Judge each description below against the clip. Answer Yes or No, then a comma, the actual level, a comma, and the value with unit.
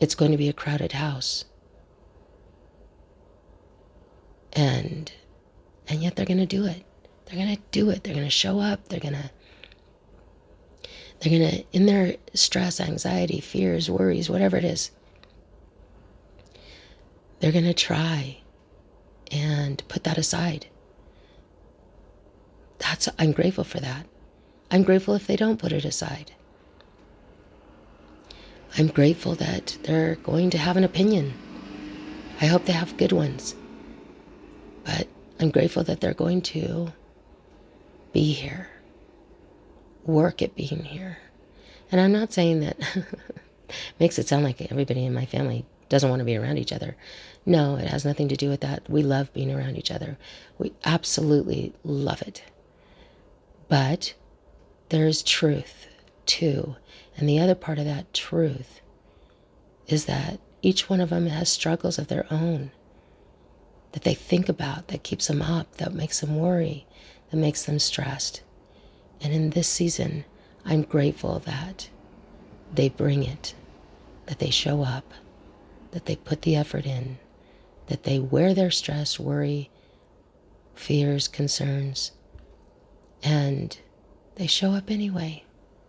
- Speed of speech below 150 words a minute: Yes, average, 140 wpm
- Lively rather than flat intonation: Yes, wide, 8.7 semitones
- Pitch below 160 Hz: Yes, medium, 150 Hz